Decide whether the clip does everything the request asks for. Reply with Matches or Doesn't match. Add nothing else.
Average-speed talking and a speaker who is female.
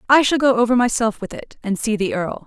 Doesn't match